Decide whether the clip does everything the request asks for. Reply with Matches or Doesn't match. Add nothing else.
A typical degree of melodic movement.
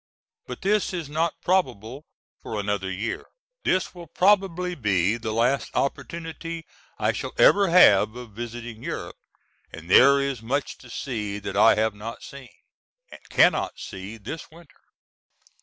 Doesn't match